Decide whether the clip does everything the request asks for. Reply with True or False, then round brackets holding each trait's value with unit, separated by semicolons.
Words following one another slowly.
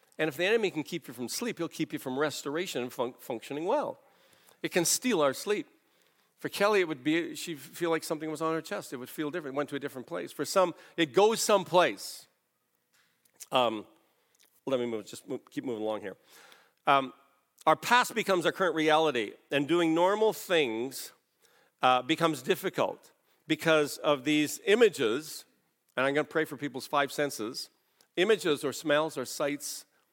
False (185 wpm)